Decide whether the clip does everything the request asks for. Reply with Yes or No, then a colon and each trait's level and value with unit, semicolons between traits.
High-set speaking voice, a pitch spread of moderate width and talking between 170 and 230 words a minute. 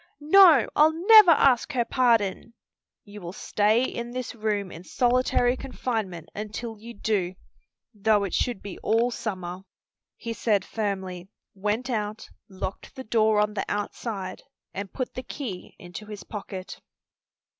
No: high, 215 Hz; average, 3.6 semitones; average, 145 wpm